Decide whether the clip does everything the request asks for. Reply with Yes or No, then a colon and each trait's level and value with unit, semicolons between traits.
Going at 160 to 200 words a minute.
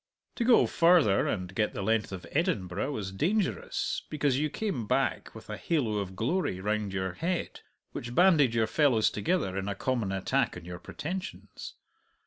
Yes: average, 170 wpm